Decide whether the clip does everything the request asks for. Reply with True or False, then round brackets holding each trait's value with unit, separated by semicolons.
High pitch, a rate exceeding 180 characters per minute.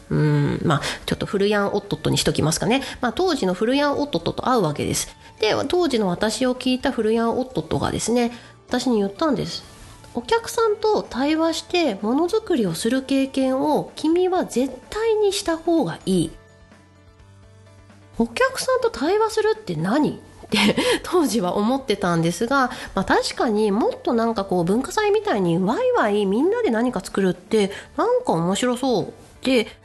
True (250 Hz; 325 characters per minute)